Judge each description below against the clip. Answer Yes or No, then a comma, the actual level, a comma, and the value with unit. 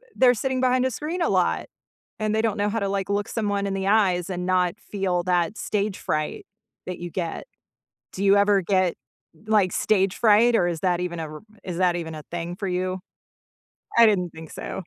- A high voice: Yes, high, 195 Hz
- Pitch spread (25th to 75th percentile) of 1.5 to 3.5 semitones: Yes, average, 3.2 semitones